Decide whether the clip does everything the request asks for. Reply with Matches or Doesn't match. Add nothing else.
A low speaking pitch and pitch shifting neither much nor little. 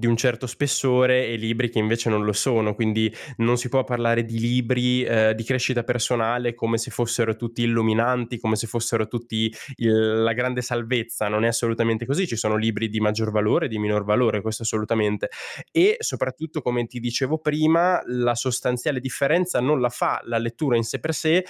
Doesn't match